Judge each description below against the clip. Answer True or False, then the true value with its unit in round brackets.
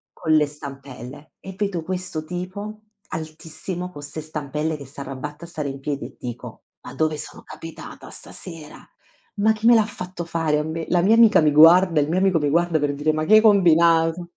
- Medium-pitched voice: True (160 Hz)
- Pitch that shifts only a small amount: False (3.4 semitones)